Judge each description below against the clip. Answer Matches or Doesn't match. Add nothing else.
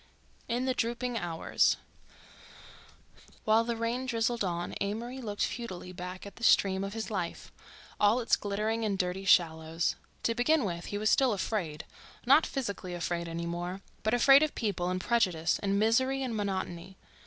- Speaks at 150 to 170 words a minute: Matches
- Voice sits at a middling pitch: Doesn't match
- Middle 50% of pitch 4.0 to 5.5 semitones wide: Matches